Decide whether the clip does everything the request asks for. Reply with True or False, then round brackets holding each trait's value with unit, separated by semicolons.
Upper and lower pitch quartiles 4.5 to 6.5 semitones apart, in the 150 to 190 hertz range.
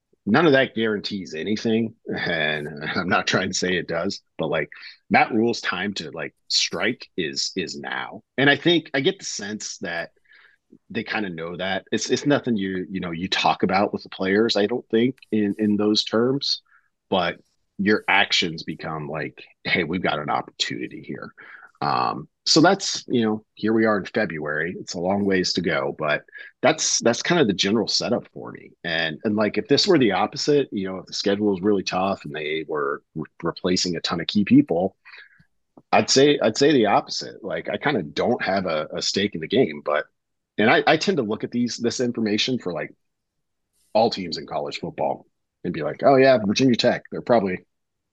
False (5.1 semitones; 110 Hz)